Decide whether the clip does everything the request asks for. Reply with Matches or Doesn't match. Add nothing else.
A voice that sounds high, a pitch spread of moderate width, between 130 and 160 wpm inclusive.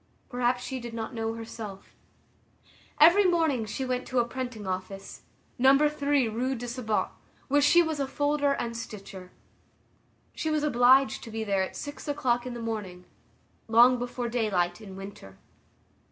Matches